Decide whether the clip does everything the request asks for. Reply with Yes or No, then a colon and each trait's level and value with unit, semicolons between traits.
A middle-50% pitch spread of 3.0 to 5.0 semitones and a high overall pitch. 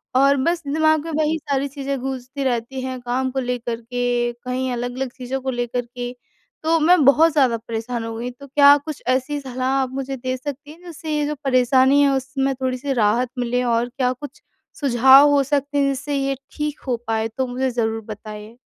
No: narrow, 2.5 semitones; very high, 260 Hz